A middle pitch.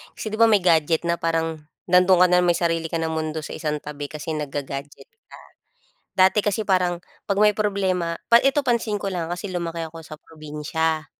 Yes: medium, 170 Hz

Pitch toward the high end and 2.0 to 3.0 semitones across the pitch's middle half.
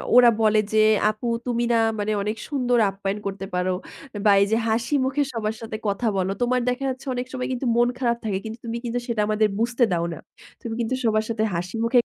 Yes: high, 225 Hz; narrow, 2.5 semitones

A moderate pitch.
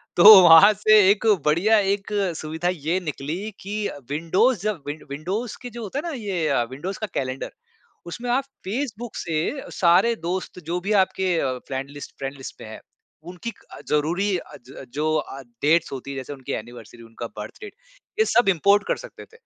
Yes: medium, 175 Hz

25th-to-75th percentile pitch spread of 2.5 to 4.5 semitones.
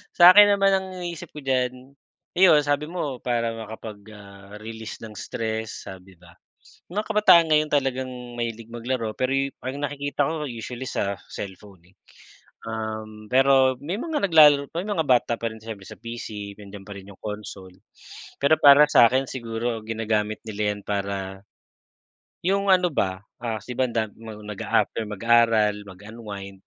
No: average, 5.1 semitones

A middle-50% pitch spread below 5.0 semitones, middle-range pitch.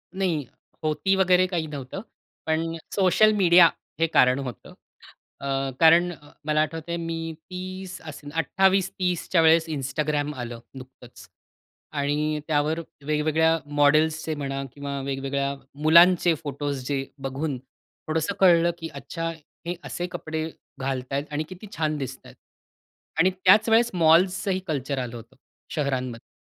Yes: average, 3.6 semitones; medium, 155 Hz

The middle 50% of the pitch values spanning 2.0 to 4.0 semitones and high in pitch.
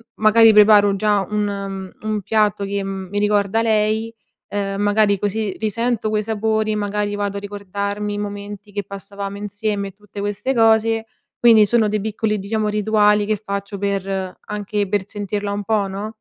No: narrow, 1.2 semitones; high, 205 Hz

